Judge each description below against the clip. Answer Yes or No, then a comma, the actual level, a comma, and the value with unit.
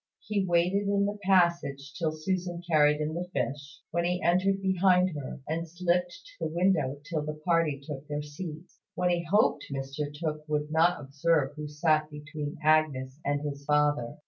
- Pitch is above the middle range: No, medium, 155 Hz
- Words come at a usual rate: Yes, average, 175 wpm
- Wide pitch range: No, average, 3.2 semitones